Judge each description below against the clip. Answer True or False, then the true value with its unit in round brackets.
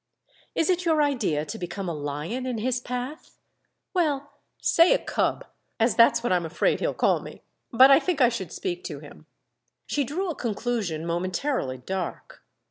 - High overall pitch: True (240 Hz)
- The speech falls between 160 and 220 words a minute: True (170 wpm)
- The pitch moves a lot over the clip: True (8.3 semitones)